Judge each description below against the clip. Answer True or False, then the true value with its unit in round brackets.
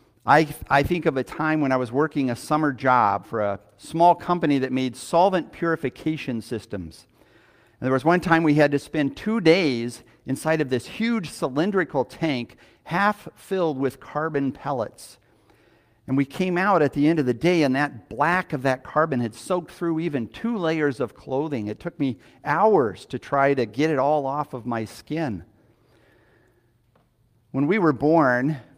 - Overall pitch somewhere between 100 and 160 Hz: True (140 Hz)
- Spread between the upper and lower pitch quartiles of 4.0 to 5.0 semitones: True (4.7 semitones)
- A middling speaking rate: True (180 wpm)